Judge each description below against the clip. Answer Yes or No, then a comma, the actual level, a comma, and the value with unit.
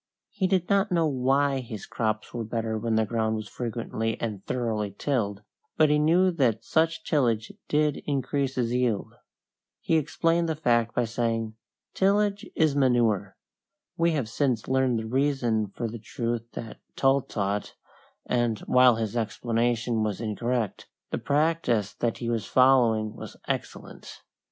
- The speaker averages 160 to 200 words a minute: No, average, 150 wpm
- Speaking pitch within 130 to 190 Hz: No, low, 120 Hz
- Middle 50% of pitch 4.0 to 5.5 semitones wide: Yes, average, 4.3 semitones